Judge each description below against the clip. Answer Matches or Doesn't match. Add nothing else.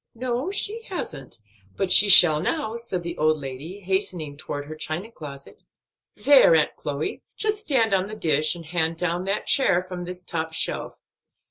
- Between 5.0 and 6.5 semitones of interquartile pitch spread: Matches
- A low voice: Doesn't match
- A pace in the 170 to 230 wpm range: Matches